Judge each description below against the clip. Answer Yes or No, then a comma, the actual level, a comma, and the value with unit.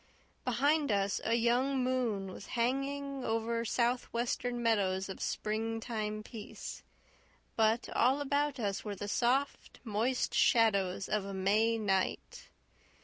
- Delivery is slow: Yes, slow, 125 wpm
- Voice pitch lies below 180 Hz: No, high, 230 Hz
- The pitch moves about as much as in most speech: Yes, average, 3.5 semitones